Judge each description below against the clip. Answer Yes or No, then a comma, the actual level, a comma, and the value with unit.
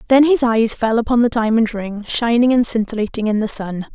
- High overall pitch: Yes, high, 230 Hz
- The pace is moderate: No, fast, 215 wpm